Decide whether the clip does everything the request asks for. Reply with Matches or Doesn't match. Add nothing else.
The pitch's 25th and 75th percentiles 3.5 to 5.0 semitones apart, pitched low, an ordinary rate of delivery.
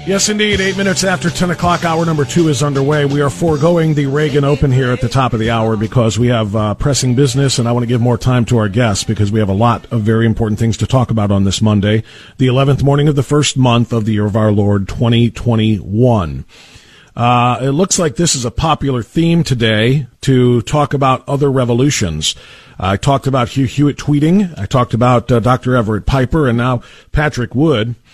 Doesn't match